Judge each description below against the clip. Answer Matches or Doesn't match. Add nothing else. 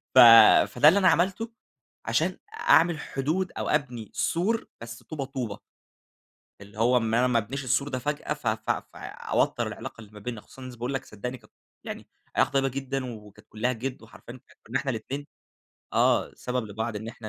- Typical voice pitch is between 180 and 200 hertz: Doesn't match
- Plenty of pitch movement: Doesn't match